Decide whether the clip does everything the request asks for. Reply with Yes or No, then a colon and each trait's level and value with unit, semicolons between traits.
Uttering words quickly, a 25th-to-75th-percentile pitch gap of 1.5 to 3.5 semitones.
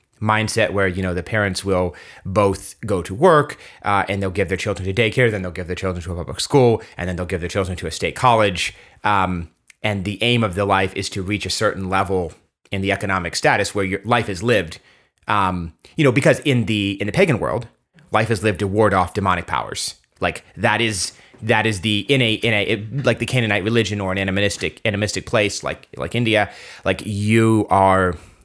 Yes: fast, 220 wpm; average, 2.7 semitones